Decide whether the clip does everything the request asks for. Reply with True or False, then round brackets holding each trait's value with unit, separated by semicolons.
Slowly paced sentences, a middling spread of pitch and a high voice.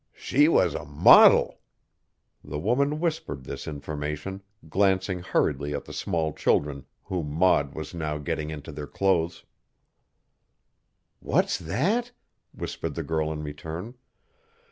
False (120 wpm; 4.6 semitones; 80 Hz)